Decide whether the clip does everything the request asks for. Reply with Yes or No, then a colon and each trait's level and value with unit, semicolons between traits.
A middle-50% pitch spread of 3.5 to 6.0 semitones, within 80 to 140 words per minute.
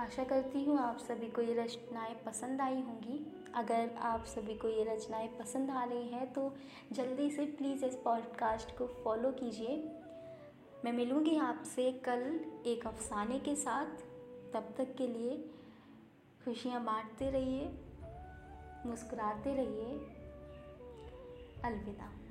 No: average, 2.7 semitones; average, 130 wpm